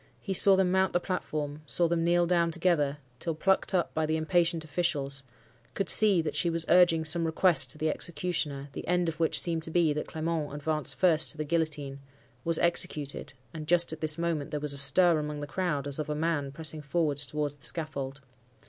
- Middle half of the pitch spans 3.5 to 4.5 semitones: No, narrow, 2.6 semitones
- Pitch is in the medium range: Yes, medium, 160 Hz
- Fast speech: Yes, fast, 210 wpm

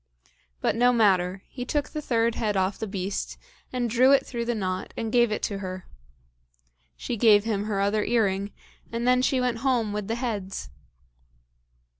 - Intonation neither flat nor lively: Yes, average, 3.4 semitones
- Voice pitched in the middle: No, high, 220 Hz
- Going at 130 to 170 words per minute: No, average, 180 wpm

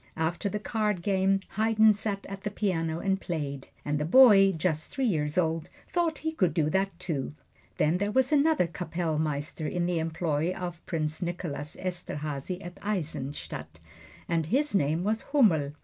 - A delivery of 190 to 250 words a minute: No, average, 165 wpm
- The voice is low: No, medium, 175 Hz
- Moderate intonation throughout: Yes, average, 4.5 semitones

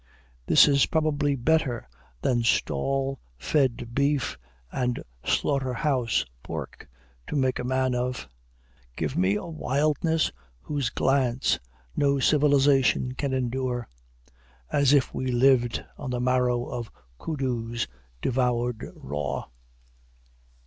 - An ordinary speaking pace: No, slow, 110 wpm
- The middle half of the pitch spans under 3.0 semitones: Yes, narrow, 2.4 semitones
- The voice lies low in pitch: Yes, low, 130 Hz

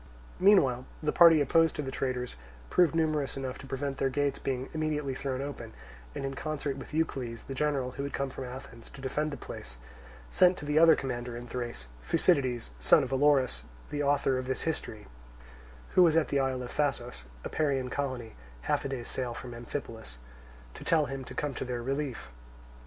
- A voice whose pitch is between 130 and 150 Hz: Yes, low, 135 Hz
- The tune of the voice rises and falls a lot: No, average, 2.9 semitones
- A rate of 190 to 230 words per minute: Yes, average, 195 wpm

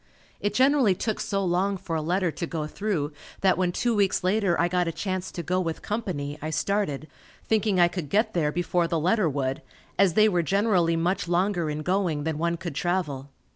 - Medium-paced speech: No, fast, 210 wpm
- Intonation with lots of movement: No, average, 3.4 semitones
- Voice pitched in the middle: Yes, medium, 180 Hz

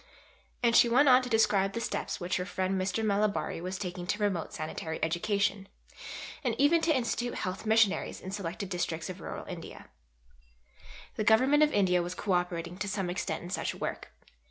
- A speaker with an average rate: Yes, average, 180 wpm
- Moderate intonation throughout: Yes, average, 3.7 semitones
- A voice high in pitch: Yes, high, 195 Hz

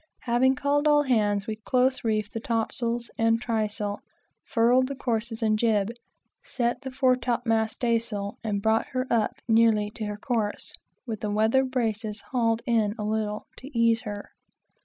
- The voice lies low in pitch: No, high, 225 Hz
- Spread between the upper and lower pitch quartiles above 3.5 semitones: No, narrow, 2.5 semitones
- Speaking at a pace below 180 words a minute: Yes, average, 165 wpm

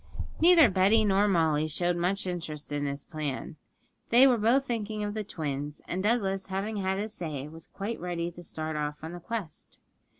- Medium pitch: Yes, medium, 180 Hz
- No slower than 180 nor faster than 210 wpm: Yes, average, 190 wpm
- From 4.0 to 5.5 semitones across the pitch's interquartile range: Yes, average, 5.1 semitones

